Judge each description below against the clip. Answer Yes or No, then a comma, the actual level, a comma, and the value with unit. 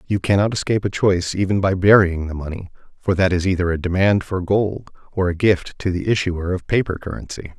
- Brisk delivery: Yes, fast, 215 wpm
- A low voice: Yes, very low, 95 Hz